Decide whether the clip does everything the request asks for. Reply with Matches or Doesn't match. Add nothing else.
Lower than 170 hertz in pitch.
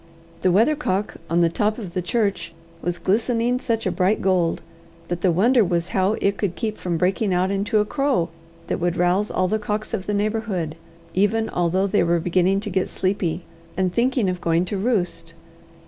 Doesn't match